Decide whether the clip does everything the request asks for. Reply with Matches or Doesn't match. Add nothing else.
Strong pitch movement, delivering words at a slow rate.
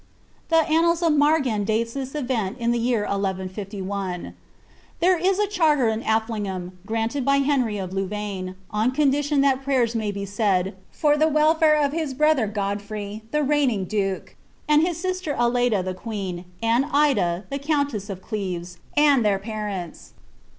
Doesn't match